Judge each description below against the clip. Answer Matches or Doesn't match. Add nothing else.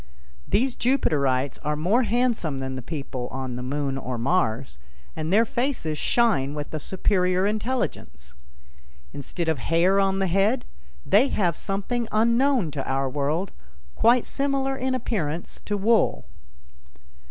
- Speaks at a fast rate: Doesn't match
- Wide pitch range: Matches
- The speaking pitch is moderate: Matches